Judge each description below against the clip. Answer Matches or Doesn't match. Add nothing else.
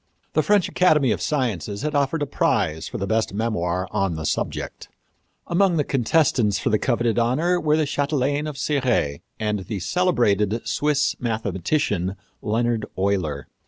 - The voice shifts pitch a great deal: Matches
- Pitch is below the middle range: Matches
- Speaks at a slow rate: Doesn't match